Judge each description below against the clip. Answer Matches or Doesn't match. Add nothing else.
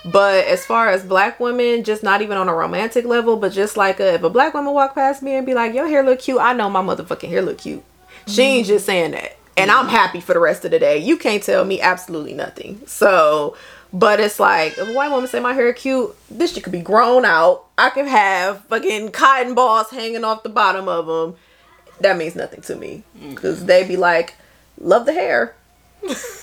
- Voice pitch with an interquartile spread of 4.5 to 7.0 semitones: Matches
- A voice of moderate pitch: Doesn't match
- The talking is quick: Matches